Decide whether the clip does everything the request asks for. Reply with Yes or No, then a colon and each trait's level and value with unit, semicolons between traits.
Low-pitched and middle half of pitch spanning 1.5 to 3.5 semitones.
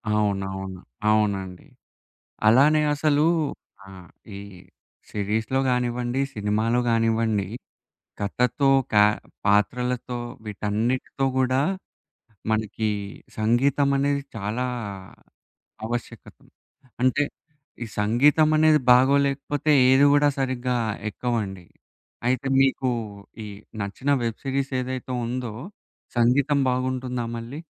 No: low, 125 Hz; average, 3.9 semitones